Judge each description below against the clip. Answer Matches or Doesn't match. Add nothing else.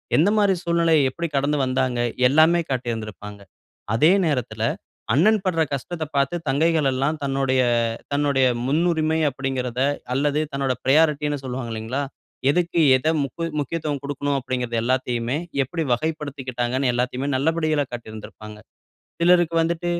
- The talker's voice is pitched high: Doesn't match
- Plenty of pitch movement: Doesn't match